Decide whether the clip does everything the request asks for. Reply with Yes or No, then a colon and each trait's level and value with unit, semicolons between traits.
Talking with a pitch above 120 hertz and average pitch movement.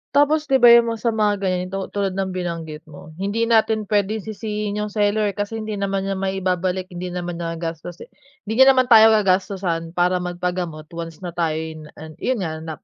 Yes: high, 190 Hz; average, 3.5 semitones